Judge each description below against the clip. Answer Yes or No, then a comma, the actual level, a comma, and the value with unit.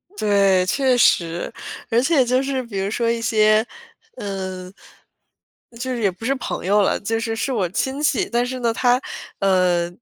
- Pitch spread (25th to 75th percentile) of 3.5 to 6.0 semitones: Yes, average, 4.4 semitones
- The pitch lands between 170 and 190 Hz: No, high, 225 Hz